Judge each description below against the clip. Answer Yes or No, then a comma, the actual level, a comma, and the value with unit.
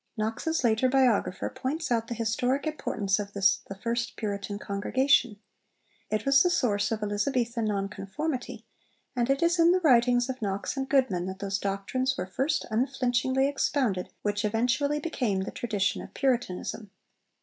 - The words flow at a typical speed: Yes, average, 160 wpm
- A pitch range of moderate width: Yes, average, 4.7 semitones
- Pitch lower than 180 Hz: No, high, 235 Hz